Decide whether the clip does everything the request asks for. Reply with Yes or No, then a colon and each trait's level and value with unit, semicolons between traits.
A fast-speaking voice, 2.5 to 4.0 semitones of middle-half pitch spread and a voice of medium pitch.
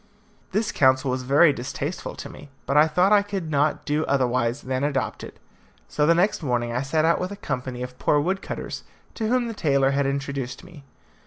No: fast, 210 wpm; average, 4.7 semitones; medium, 145 Hz